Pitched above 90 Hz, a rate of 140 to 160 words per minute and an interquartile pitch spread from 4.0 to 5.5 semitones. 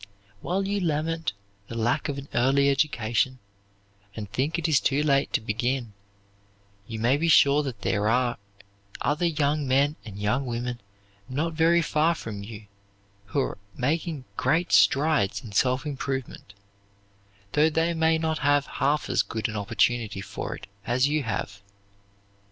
Yes: low, 135 Hz; average, 150 wpm; average, 4.8 semitones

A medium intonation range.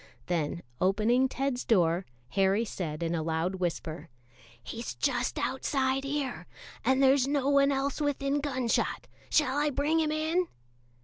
No: wide, 7.4 semitones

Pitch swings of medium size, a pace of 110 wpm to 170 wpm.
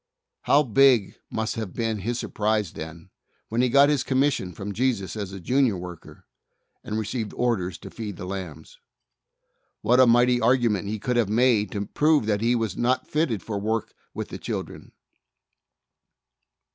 Yes: average, 3.8 semitones; average, 165 wpm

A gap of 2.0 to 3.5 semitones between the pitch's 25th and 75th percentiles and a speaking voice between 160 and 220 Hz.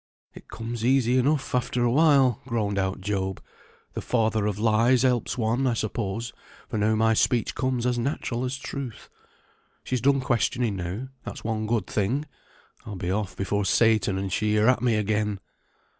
No: average, 3.1 semitones; low, 115 Hz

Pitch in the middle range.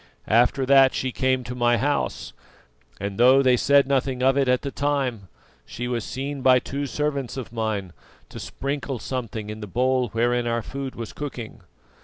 No: low, 125 Hz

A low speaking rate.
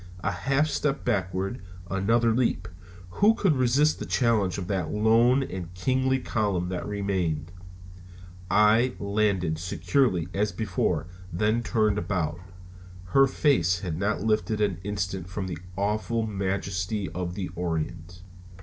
Yes: slow, 130 wpm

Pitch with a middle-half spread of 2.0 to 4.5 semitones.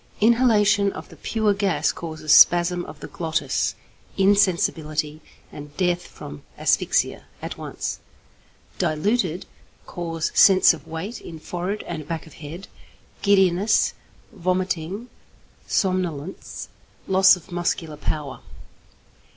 Yes: average, 3.7 semitones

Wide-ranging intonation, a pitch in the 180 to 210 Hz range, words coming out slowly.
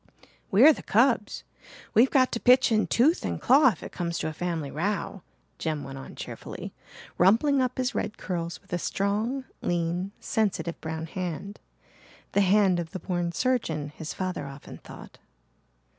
No: wide, 5.8 semitones; high, 190 Hz; average, 165 wpm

